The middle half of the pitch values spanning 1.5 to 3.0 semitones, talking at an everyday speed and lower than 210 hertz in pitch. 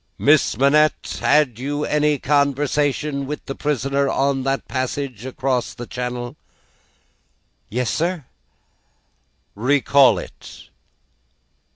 No: narrow, 2.5 semitones; slow, 95 wpm; medium, 140 Hz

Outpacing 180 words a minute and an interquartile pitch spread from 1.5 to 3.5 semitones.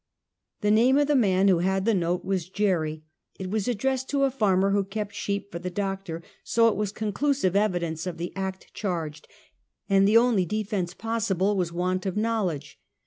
Yes: average, 190 wpm; average, 3.1 semitones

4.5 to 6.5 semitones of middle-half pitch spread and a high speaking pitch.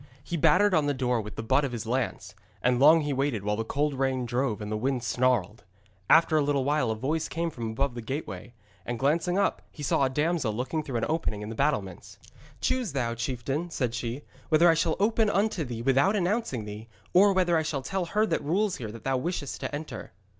No: wide, 5.5 semitones; low, 135 Hz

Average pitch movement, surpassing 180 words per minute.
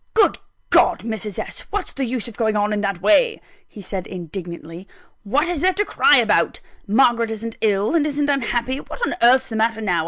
Yes: average, 5.0 semitones; fast, 205 wpm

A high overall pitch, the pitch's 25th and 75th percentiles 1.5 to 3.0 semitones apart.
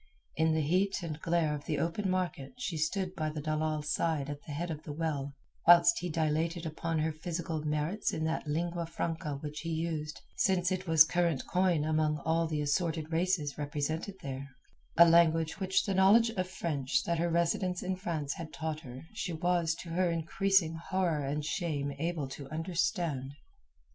No: medium, 160 Hz; narrow, 2.4 semitones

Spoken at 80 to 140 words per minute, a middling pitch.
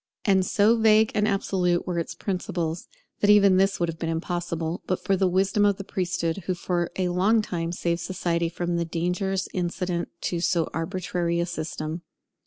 No: average, 185 wpm; medium, 180 Hz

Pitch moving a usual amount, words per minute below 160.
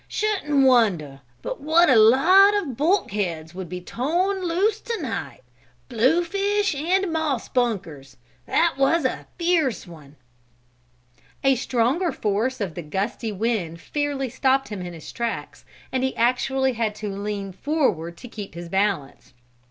No: wide, 8.5 semitones; average, 145 wpm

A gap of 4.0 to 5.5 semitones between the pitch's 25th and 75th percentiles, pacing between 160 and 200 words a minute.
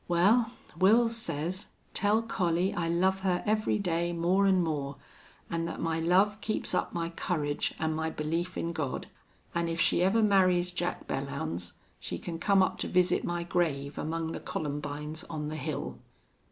No: average, 3.2 semitones; average, 170 wpm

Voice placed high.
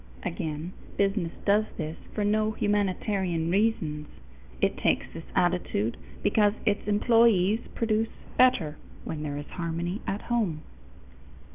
Yes: high, 195 Hz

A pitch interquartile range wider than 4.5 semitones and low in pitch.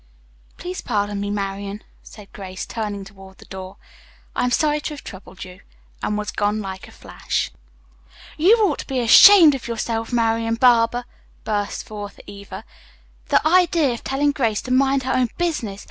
No: average, 5.0 semitones; high, 225 Hz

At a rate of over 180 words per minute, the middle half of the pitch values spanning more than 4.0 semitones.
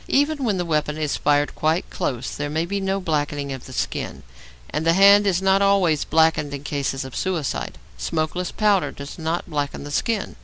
Yes: average, 195 wpm; average, 4.8 semitones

